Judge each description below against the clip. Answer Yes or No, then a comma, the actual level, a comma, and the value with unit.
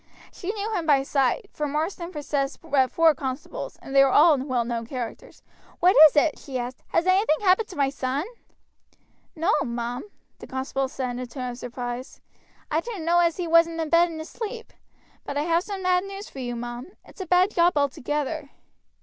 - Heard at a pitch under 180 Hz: No, very high, 300 Hz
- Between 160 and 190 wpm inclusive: No, average, 200 wpm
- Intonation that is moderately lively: Yes, average, 5.0 semitones